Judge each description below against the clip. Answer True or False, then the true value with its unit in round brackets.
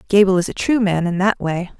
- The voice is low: False (190 Hz)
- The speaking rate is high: True (265 wpm)